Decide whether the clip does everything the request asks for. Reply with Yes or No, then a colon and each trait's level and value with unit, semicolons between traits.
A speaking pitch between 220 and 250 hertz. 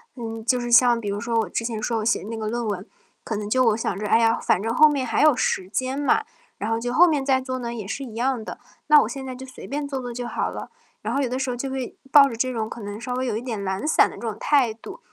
Yes: high, 240 Hz